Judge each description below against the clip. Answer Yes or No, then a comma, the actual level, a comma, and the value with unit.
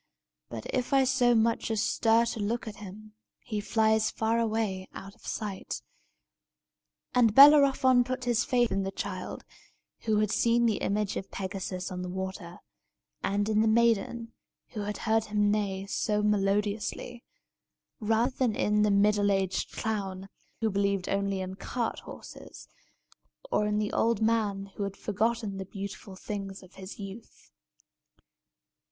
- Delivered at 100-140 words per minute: No, average, 155 wpm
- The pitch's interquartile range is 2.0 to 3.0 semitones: Yes, narrow, 2.6 semitones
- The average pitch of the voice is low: No, high, 210 Hz